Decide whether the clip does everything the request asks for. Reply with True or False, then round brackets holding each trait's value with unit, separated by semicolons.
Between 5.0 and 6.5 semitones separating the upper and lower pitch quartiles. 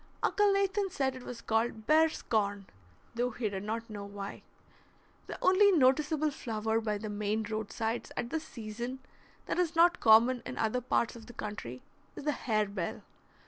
True (5.5 semitones)